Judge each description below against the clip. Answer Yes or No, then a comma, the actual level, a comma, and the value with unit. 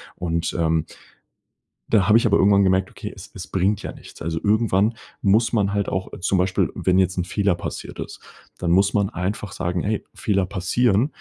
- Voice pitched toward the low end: Yes, very low, 95 Hz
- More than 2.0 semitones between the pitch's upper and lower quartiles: Yes, narrow, 2.4 semitones